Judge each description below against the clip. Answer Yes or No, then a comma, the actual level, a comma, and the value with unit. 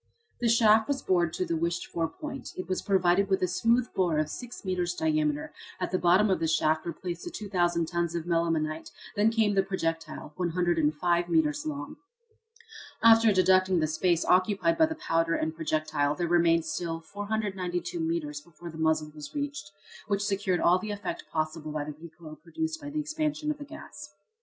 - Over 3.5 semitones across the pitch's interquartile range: Yes, average, 4.0 semitones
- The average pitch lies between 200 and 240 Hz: No, medium, 175 Hz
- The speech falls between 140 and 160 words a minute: No, average, 185 wpm